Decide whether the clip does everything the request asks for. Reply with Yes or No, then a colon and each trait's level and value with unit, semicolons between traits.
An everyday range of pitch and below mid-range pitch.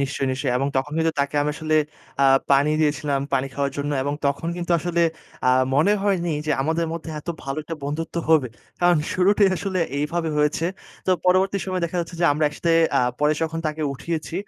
No: average, 3.1 semitones; medium, 160 Hz